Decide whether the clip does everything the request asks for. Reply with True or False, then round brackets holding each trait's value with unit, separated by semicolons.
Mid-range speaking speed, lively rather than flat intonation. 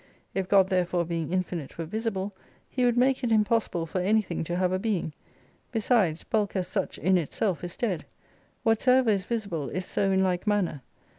False (180 wpm; 3.7 semitones)